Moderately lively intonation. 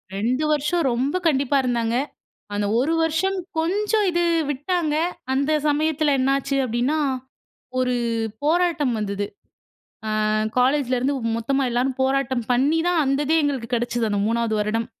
Yes: average, 4.4 semitones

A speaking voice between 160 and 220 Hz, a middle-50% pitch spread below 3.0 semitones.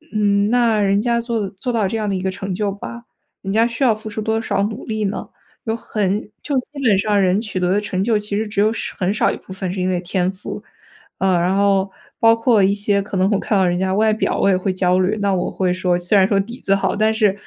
Yes: high, 200 Hz; narrow, 2.4 semitones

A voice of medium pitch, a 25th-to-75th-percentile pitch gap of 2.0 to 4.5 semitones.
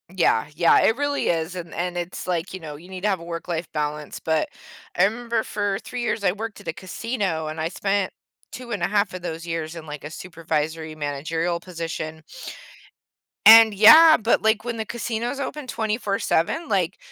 No: medium, 180 Hz; average, 5.2 semitones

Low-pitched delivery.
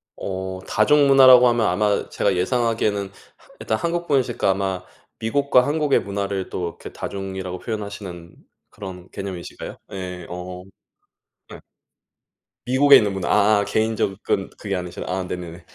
Yes: low, 100 Hz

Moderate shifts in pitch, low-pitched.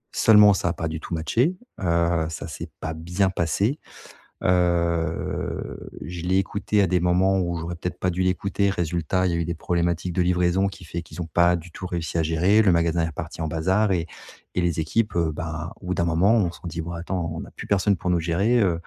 No: narrow, 2.1 semitones; very low, 85 Hz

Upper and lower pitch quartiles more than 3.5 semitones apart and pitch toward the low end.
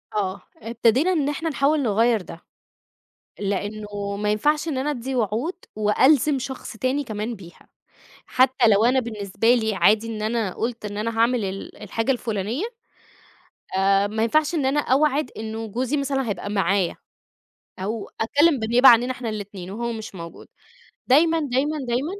No: average, 4.3 semitones; high, 230 Hz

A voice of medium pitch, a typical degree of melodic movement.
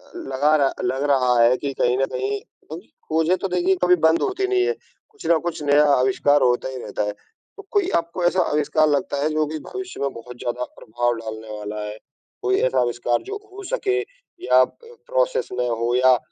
No: medium, 145 Hz; wide, 6.8 semitones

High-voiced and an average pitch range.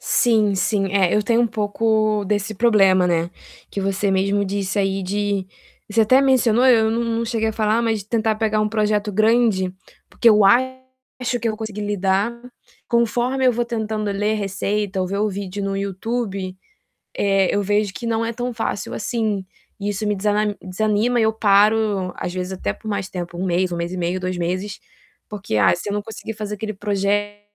No: high, 210 Hz; narrow, 2.3 semitones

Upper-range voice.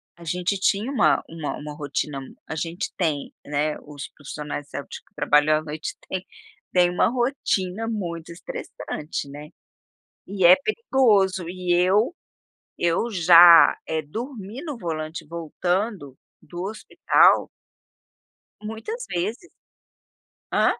No: medium, 175 Hz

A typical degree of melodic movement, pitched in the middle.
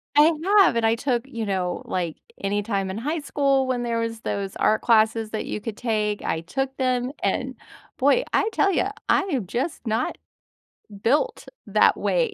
No: average, 4.4 semitones; high, 230 Hz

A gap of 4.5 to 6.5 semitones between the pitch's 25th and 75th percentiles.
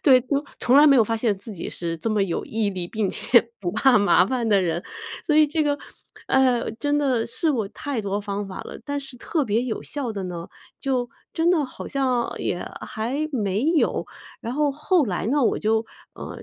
Yes: wide, 5.5 semitones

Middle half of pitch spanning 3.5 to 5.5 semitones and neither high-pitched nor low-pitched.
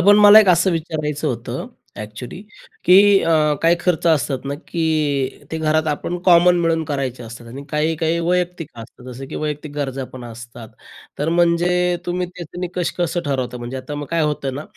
Yes: average, 4.3 semitones; medium, 155 Hz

